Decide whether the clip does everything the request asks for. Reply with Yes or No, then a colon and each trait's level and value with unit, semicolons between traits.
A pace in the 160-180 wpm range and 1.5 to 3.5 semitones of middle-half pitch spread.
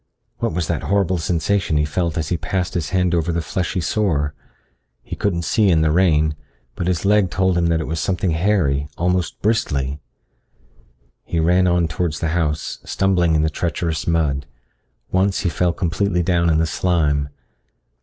Yes: average, 175 wpm; average, 2.7 semitones